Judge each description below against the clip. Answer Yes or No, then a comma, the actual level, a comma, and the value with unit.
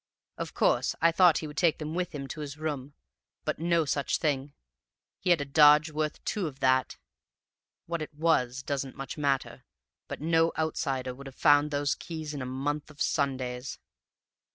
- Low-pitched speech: No, medium, 145 Hz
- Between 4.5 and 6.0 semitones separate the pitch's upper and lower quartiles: No, narrow, 2.6 semitones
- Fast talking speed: No, average, 180 wpm